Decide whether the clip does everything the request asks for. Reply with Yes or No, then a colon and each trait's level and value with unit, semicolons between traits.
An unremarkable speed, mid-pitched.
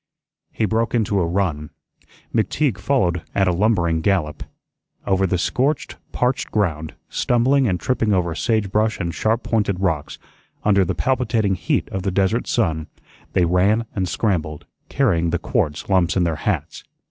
No: average, 160 wpm; very low, 95 Hz